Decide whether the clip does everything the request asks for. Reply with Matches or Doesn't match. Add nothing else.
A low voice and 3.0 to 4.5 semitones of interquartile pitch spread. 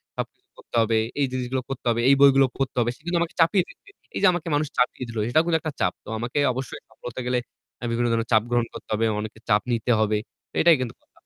Matches